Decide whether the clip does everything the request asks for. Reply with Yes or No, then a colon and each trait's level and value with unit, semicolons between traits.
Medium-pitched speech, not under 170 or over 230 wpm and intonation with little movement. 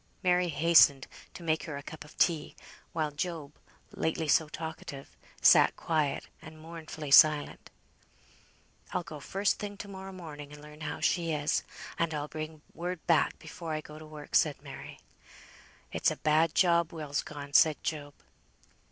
No: medium, 155 Hz; average, 160 wpm; narrow, 2.1 semitones